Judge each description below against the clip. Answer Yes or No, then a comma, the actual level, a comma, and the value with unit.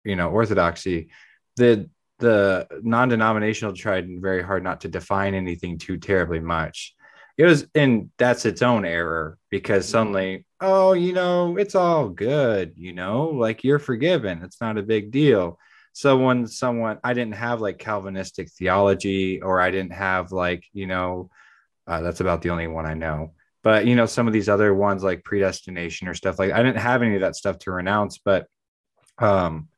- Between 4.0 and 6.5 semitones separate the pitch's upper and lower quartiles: Yes, average, 4.7 semitones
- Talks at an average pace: Yes, average, 180 wpm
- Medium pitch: No, low, 100 Hz